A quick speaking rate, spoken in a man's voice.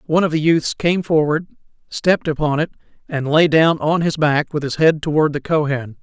Yes: fast, 210 wpm; male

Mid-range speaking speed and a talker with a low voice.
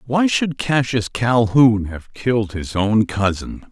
Yes: average, 145 wpm; low, 115 Hz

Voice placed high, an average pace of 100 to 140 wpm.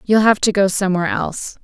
No: high, 195 Hz; fast, 220 wpm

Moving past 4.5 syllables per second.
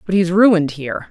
Yes: 6.1 syllables/s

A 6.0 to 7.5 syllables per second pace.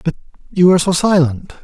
Yes: 6.4 syllables/s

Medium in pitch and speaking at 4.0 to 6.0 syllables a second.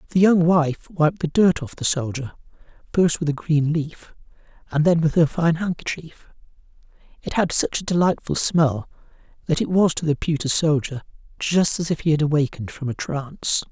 Yes: medium, 155 Hz; 5.0 syllables/s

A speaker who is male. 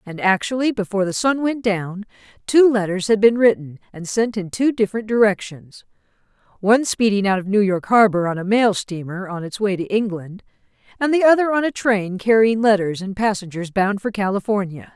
No: female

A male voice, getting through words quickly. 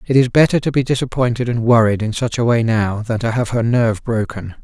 Yes: male; fast, 245 wpm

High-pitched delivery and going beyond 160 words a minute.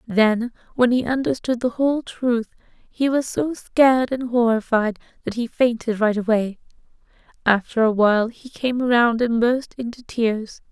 No: high, 235 Hz; average, 155 wpm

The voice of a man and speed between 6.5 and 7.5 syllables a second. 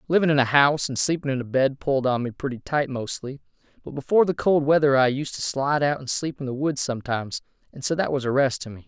Yes: male; 6.6 syllables/s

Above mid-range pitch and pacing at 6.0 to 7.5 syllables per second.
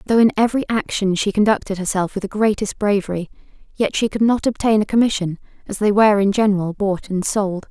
Yes: high, 205 Hz; 6.1 syllables/s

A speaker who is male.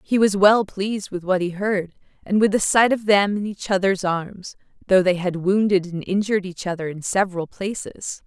No: female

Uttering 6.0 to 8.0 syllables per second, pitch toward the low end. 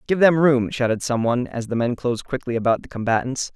Yes: 6.2 syllables/s; low, 125 Hz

